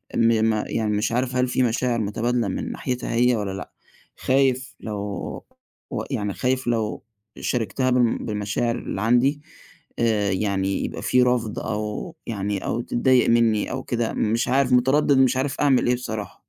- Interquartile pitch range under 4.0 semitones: Yes, average, 3.0 semitones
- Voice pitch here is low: Yes, low, 120 Hz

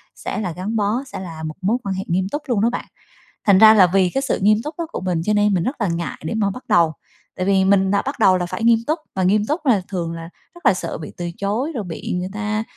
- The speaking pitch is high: Yes, high, 200 Hz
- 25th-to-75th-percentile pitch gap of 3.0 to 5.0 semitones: Yes, average, 3.4 semitones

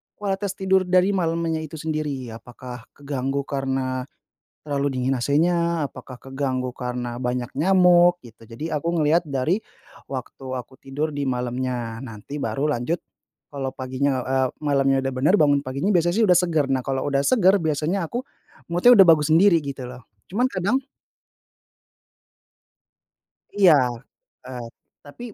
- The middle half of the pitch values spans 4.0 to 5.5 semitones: Yes, average, 4.6 semitones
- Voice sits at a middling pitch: Yes, medium, 145 Hz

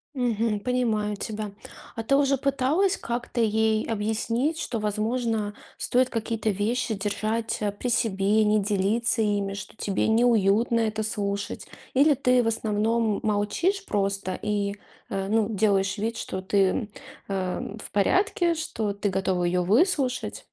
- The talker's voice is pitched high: Yes, high, 220 Hz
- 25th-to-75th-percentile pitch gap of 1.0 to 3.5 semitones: Yes, average, 2.8 semitones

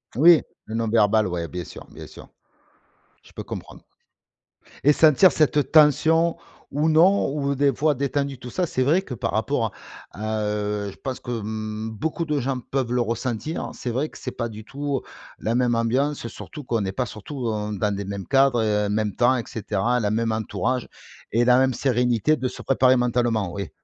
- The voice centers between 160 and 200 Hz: No, low, 120 Hz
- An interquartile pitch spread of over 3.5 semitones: Yes, average, 4.3 semitones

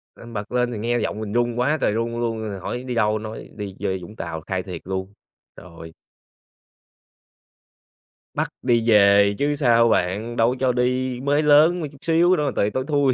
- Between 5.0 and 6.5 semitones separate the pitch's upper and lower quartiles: No, average, 4.0 semitones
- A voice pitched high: No, low, 115 Hz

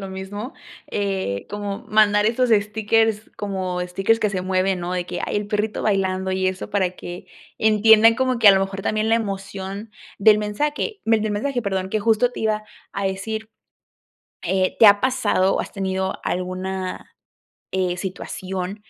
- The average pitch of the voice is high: Yes, high, 200 Hz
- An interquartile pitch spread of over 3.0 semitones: No, narrow, 2.4 semitones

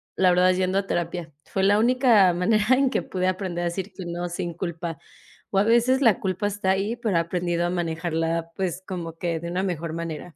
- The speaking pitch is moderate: Yes, medium, 180 Hz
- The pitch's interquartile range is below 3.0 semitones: Yes, narrow, 2.5 semitones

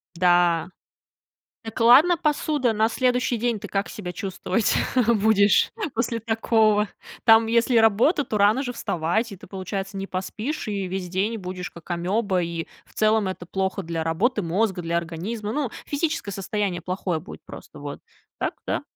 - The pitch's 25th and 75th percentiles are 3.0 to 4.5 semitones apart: Yes, average, 4.0 semitones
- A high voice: Yes, high, 205 Hz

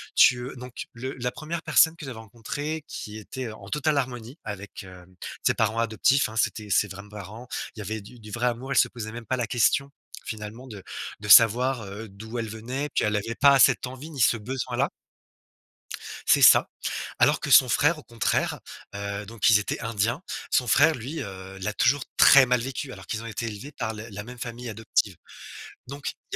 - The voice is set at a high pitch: No, low, 115 Hz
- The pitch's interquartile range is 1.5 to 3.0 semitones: No, average, 3.6 semitones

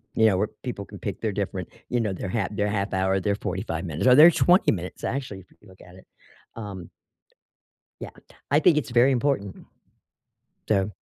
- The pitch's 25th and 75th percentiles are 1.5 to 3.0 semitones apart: No, average, 3.9 semitones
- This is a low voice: Yes, low, 100 Hz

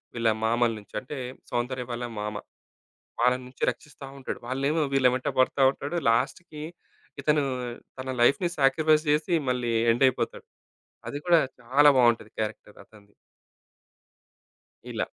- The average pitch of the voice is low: Yes, low, 130 Hz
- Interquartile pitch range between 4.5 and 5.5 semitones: No, average, 3.8 semitones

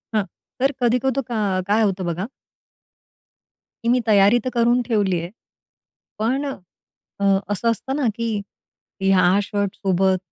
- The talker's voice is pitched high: Yes, high, 210 Hz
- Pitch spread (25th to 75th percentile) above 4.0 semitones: No, average, 3.7 semitones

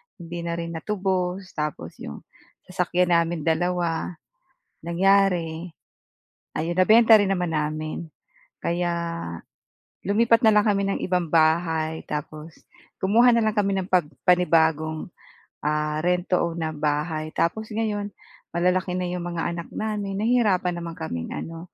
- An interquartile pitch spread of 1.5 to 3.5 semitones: Yes, average, 3.2 semitones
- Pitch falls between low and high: Yes, medium, 175 Hz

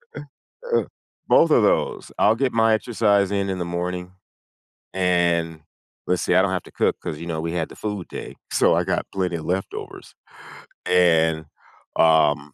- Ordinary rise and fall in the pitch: Yes, average, 3.0 semitones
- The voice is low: Yes, very low, 90 Hz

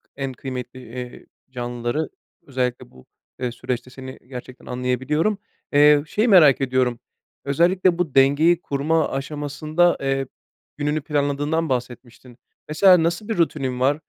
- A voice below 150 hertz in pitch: Yes, medium, 140 Hz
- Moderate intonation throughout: Yes, average, 3.6 semitones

